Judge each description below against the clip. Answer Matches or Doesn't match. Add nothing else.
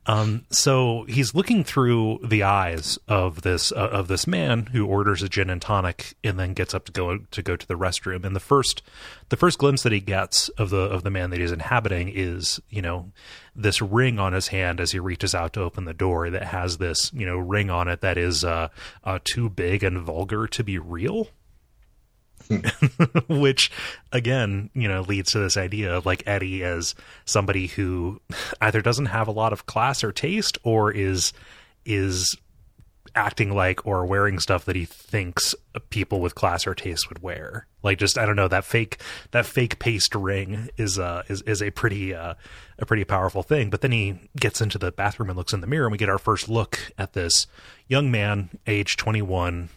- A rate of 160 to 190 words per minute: Doesn't match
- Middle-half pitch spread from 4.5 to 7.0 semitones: Doesn't match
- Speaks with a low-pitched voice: Matches